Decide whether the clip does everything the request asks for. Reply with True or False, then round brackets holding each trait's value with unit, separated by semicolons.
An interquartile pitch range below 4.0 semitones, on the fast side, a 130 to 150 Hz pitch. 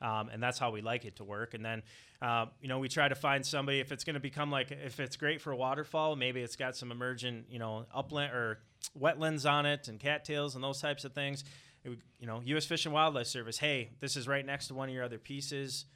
True (2.9 semitones; 260 wpm; 135 Hz)